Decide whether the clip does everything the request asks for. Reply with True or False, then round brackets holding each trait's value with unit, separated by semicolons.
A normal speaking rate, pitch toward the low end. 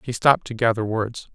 False (220 wpm; 115 Hz)